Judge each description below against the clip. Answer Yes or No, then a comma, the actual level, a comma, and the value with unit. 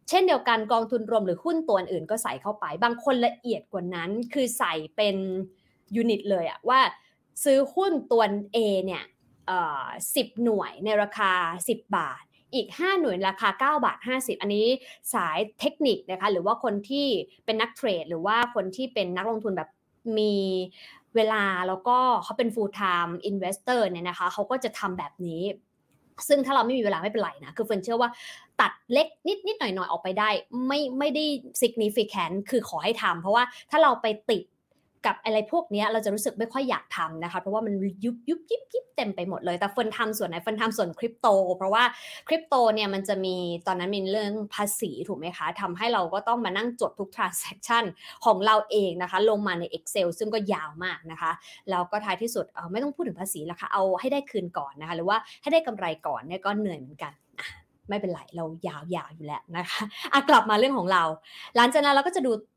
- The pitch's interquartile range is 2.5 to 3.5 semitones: No, average, 4.4 semitones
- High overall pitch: Yes, high, 215 Hz